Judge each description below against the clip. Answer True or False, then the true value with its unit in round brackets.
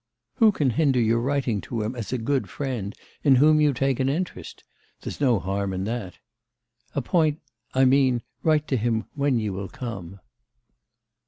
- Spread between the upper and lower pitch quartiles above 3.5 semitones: True (4.4 semitones)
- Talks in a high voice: False (125 Hz)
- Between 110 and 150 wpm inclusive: False (170 wpm)